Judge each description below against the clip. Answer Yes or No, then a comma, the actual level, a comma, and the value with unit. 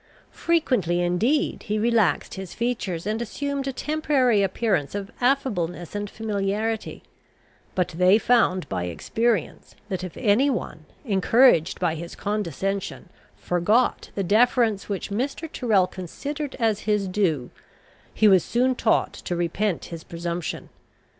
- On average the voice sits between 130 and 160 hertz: No, high, 205 Hz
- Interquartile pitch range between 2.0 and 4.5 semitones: No, average, 5.1 semitones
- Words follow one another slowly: Yes, slow, 130 wpm